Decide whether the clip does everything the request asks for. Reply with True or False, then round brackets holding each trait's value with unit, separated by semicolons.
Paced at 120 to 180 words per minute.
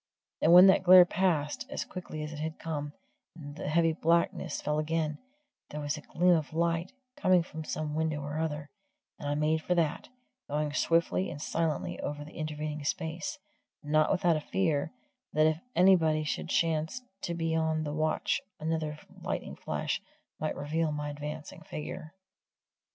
True (165 wpm)